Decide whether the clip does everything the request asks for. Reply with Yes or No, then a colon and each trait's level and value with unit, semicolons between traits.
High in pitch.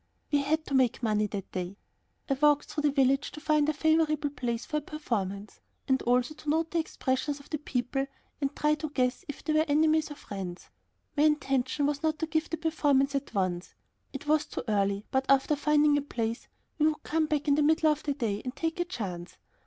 Yes: very high, 285 Hz